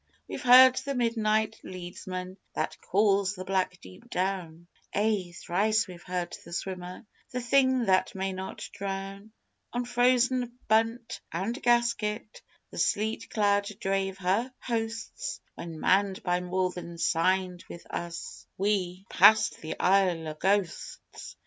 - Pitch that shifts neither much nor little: Yes, average, 3.6 semitones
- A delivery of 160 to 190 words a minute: No, slow, 135 wpm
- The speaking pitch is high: Yes, high, 195 Hz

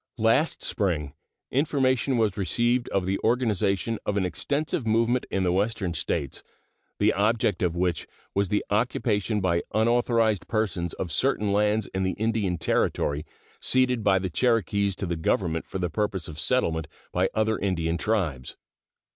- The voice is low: Yes, low, 100 Hz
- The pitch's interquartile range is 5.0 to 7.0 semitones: No, average, 4.3 semitones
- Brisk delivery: No, average, 155 wpm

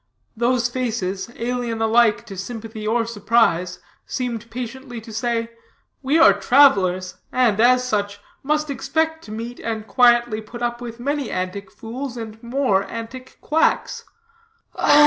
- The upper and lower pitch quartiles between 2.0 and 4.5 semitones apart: Yes, average, 2.7 semitones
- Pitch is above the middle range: Yes, high, 235 Hz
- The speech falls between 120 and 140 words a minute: Yes, slow, 135 wpm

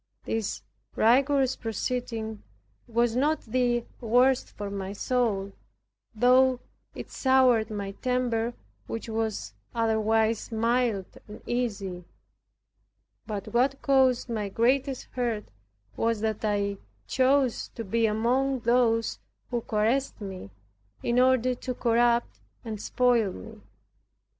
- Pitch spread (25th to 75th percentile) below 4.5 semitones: Yes, narrow, 2.6 semitones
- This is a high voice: Yes, high, 230 Hz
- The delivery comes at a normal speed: No, slow, 110 wpm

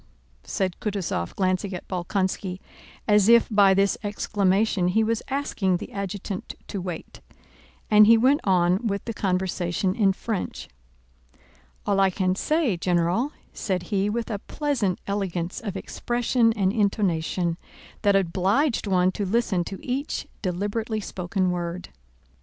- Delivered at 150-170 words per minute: No, slow, 135 wpm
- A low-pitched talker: No, high, 195 Hz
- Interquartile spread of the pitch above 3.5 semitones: No, average, 3.0 semitones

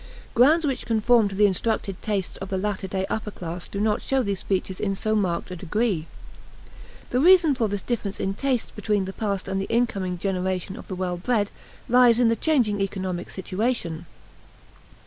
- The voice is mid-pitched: No, high, 205 Hz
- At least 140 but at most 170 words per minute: No, average, 185 wpm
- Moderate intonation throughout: Yes, average, 3.6 semitones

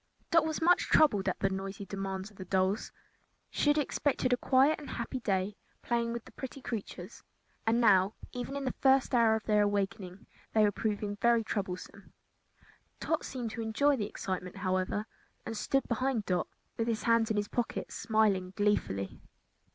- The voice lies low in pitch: No, high, 220 Hz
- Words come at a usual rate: Yes, average, 175 wpm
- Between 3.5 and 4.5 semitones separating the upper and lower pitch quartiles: Yes, average, 4.1 semitones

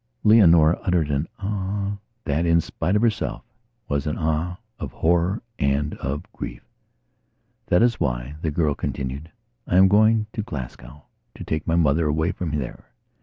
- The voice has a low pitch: Yes, very low, 80 Hz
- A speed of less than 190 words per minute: Yes, average, 155 wpm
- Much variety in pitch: No, average, 4.6 semitones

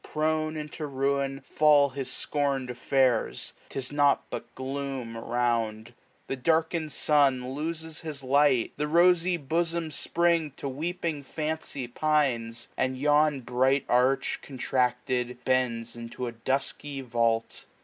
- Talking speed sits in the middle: No, slow, 125 wpm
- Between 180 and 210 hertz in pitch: No, low, 135 Hz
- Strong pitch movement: No, average, 3.4 semitones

